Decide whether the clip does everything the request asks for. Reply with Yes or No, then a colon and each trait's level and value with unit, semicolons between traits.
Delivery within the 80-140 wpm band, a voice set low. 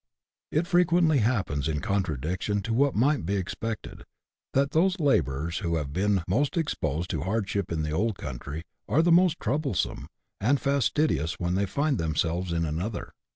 No: average, 170 wpm; low, 100 Hz